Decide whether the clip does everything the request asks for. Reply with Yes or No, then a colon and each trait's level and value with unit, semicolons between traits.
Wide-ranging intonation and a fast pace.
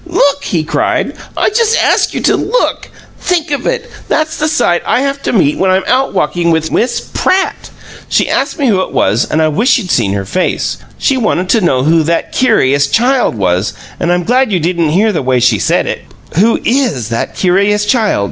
Yes: wide, 8.7 semitones; fast, 210 wpm